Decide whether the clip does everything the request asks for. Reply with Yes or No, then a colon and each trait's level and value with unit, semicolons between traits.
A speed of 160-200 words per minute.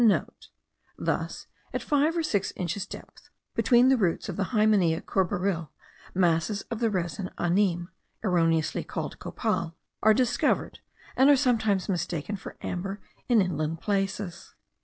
No: average, 140 wpm